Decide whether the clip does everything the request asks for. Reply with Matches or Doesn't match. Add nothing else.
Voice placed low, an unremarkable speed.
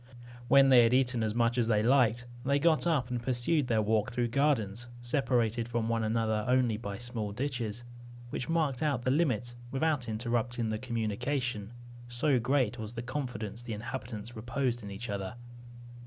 Matches